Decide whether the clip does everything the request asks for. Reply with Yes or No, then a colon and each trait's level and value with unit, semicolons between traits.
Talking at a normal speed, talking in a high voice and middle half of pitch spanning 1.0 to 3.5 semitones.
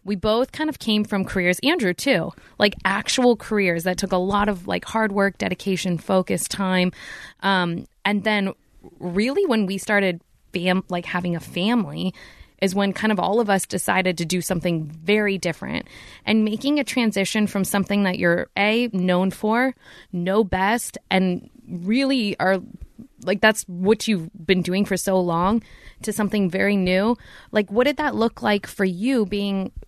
Yes: average, 175 wpm; high, 195 Hz; average, 2.9 semitones